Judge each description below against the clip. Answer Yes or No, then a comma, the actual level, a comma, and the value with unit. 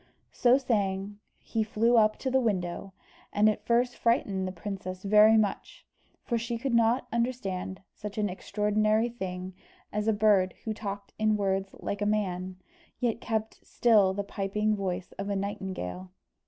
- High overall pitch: Yes, high, 210 Hz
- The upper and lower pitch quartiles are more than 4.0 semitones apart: No, narrow, 2.6 semitones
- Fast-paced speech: No, average, 160 wpm